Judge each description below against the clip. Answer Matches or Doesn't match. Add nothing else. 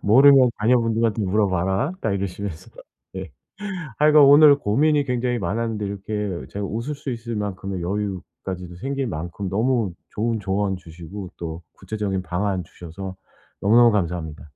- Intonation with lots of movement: Doesn't match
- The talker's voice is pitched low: Matches